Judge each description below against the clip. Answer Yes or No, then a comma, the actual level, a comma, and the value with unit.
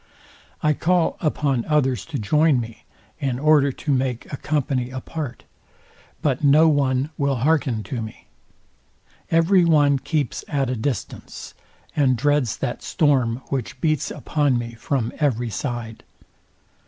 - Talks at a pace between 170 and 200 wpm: No, slow, 135 wpm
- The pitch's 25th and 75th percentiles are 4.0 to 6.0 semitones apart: No, average, 3.6 semitones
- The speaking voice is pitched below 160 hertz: Yes, low, 135 Hz